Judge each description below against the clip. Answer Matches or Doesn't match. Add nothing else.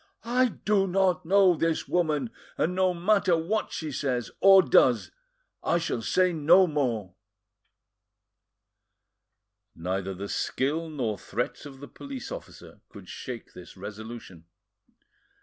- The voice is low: Doesn't match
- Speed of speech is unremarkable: Doesn't match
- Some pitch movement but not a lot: Doesn't match